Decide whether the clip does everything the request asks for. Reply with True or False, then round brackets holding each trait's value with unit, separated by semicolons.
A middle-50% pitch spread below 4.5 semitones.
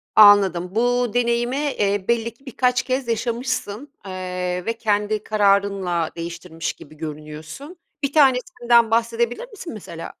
False (5.0 semitones)